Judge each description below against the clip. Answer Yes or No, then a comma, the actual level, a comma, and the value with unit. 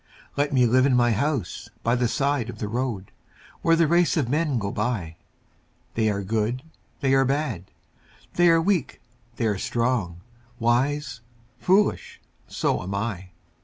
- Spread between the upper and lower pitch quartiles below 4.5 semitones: No, average, 4.9 semitones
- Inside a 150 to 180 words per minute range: Yes, average, 160 wpm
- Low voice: Yes, low, 125 Hz